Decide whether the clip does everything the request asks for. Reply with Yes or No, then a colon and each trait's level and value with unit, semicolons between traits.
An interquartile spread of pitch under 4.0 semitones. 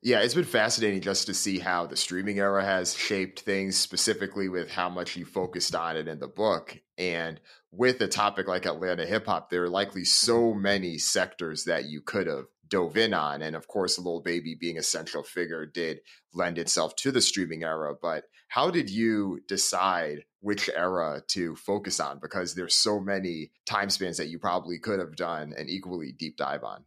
Yes: narrow, 2.5 semitones